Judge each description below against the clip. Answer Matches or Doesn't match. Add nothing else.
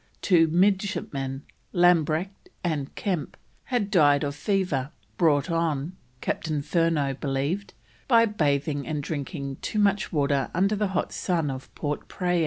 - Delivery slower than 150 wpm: Matches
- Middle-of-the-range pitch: Matches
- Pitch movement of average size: Matches